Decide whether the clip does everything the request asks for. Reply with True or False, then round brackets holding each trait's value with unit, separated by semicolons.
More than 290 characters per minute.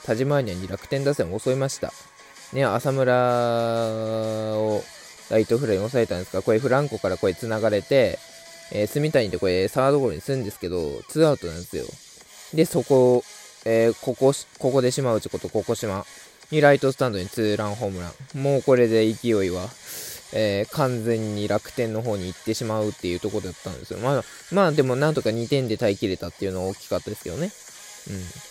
True (400 characters per minute)